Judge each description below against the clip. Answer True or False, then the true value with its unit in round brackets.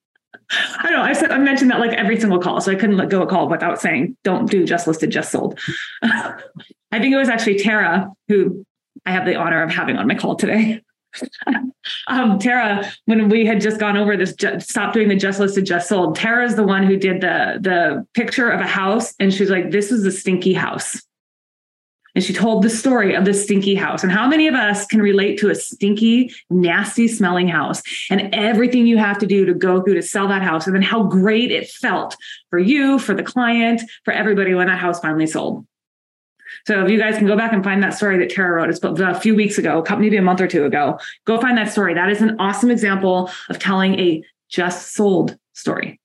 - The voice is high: True (200 Hz)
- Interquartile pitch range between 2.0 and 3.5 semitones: True (3.1 semitones)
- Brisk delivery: True (230 wpm)